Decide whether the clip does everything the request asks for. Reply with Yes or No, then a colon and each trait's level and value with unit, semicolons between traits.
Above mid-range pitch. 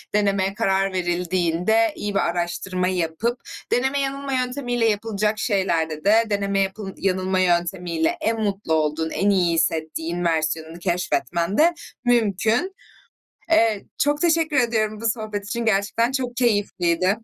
Yes: high, 200 Hz